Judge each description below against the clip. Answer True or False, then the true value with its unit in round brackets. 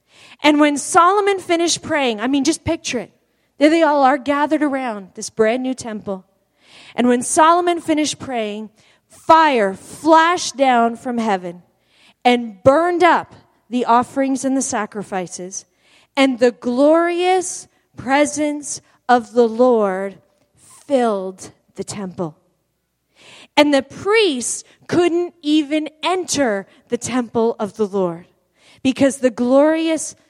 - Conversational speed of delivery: False (125 wpm)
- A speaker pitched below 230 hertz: False (260 Hz)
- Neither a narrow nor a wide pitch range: False (5.8 semitones)